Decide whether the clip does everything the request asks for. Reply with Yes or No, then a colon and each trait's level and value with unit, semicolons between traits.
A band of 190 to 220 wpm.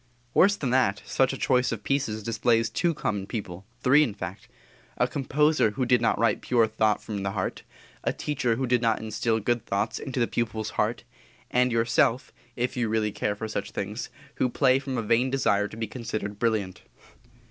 Yes: average, 195 wpm